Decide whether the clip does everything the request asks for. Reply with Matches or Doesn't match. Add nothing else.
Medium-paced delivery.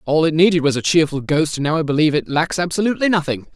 Doesn't match